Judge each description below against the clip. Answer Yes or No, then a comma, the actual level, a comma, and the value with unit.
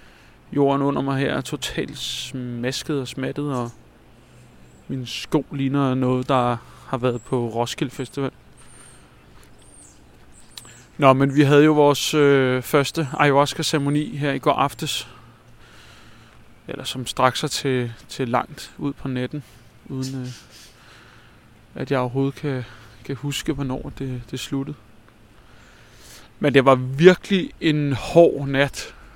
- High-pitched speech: No, low, 135 Hz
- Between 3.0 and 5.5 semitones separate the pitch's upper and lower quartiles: No, narrow, 2.5 semitones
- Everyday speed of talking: No, slow, 130 wpm